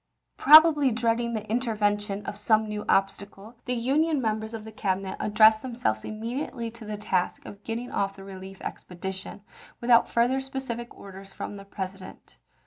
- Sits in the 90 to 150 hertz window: No, high, 220 Hz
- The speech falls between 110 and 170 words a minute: Yes, average, 160 wpm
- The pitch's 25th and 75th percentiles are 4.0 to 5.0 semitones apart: No, average, 3.3 semitones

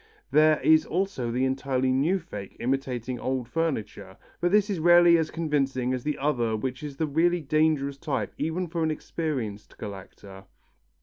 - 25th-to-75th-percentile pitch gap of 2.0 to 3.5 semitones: No, average, 4.3 semitones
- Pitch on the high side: No, medium, 140 Hz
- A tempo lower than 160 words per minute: No, average, 165 wpm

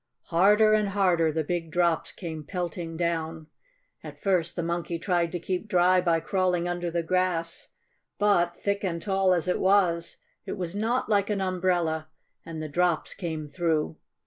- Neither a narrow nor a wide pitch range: No, narrow, 2.1 semitones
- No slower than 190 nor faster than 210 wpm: No, average, 170 wpm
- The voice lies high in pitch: No, medium, 175 Hz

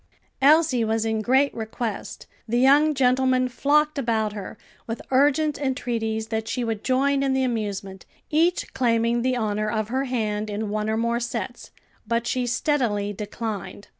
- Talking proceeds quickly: No, average, 160 wpm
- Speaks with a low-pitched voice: No, high, 235 Hz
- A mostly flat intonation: No, average, 3.4 semitones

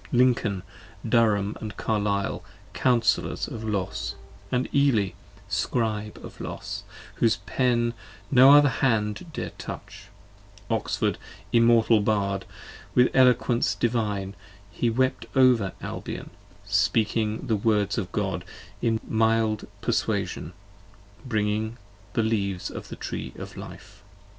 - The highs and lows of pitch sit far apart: No, narrow, 2.5 semitones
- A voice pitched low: Yes, low, 110 Hz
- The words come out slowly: Yes, slow, 110 wpm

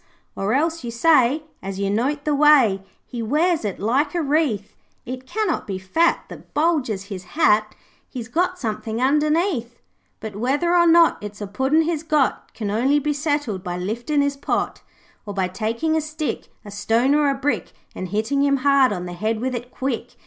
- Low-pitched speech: No, very high, 260 Hz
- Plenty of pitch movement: Yes, wide, 5.9 semitones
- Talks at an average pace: Yes, average, 190 wpm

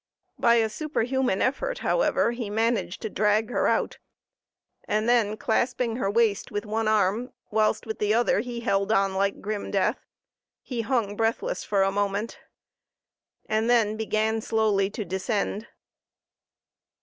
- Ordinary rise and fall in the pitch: No, narrow, 2.3 semitones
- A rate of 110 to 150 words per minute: Yes, average, 145 wpm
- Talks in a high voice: Yes, high, 220 Hz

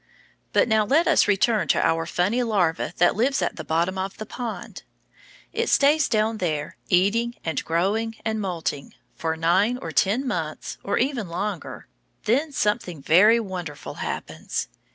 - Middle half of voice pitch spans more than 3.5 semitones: Yes, average, 5.2 semitones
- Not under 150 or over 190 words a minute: Yes, average, 155 wpm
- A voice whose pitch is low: No, high, 200 Hz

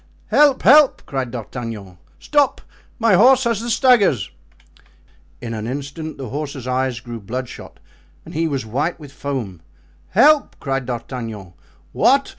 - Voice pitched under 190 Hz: Yes, low, 135 Hz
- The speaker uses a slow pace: Yes, slow, 130 wpm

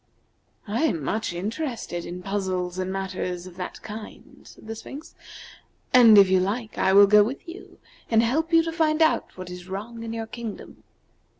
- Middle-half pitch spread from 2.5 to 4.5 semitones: Yes, average, 4.2 semitones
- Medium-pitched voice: No, high, 210 Hz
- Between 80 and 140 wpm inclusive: No, average, 180 wpm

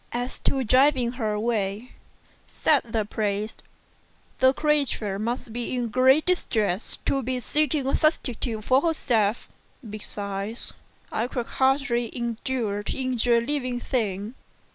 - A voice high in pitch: Yes, high, 240 Hz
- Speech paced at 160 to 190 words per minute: No, slow, 135 wpm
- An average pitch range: Yes, average, 3.5 semitones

